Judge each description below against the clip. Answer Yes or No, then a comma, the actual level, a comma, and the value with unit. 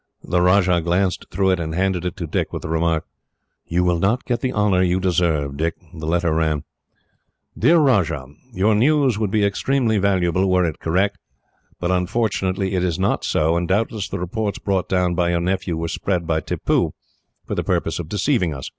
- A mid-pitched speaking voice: No, very low, 90 Hz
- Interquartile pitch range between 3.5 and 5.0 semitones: No, average, 2.9 semitones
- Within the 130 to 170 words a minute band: No, average, 195 wpm